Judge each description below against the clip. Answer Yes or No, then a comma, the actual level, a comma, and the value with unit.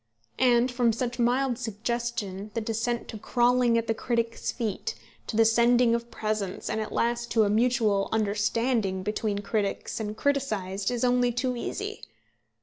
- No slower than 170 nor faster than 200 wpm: No, average, 155 wpm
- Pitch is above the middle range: Yes, high, 230 Hz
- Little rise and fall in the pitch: Yes, narrow, 2.2 semitones